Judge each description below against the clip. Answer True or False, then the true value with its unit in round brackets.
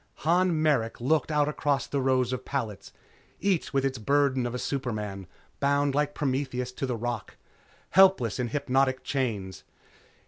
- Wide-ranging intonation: False (3.0 semitones)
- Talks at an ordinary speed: True (150 wpm)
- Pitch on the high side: False (135 Hz)